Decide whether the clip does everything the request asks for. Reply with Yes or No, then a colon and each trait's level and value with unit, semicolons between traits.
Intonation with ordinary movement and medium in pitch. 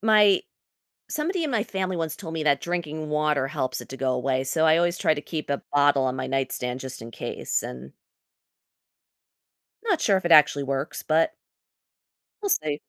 Yes: average, 4.7 semitones; medium, 155 Hz